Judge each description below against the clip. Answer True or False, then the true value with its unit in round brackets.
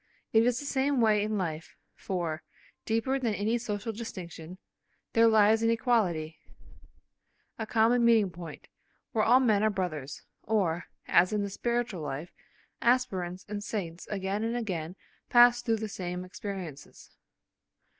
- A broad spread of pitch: False (4.3 semitones)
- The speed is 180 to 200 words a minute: False (145 wpm)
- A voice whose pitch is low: False (210 Hz)